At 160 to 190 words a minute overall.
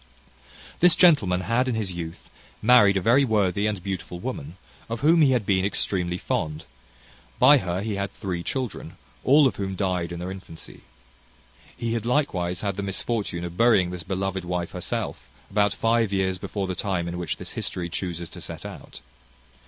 Yes: average, 180 wpm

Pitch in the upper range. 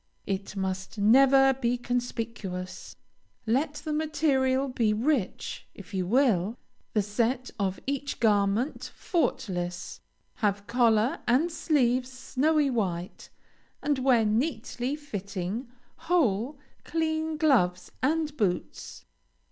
Yes: high, 245 Hz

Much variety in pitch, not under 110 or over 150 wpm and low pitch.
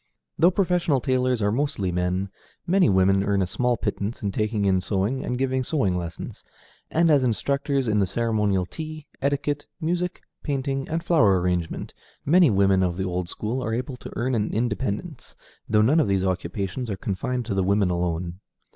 No: wide, 6.3 semitones; average, 180 wpm; low, 110 Hz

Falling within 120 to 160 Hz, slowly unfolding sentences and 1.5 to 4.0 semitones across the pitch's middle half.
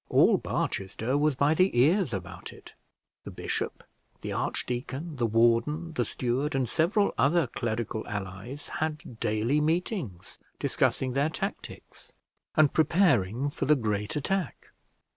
No: low, 135 Hz; slow, 130 wpm; wide, 5.4 semitones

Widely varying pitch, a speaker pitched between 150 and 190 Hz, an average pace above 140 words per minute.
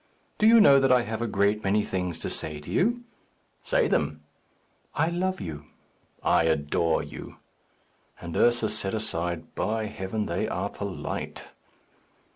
No: wide, 7.1 semitones; low, 105 Hz; average, 150 wpm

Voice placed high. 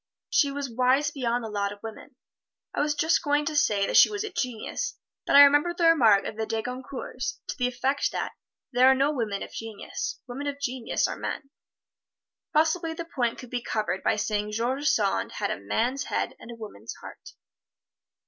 Yes: very high, 255 Hz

